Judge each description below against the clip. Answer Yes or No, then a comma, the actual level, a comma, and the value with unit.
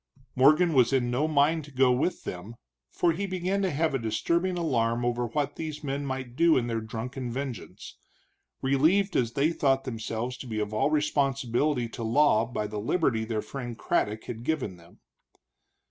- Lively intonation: No, average, 4.7 semitones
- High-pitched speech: No, low, 130 Hz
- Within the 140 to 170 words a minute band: No, average, 180 wpm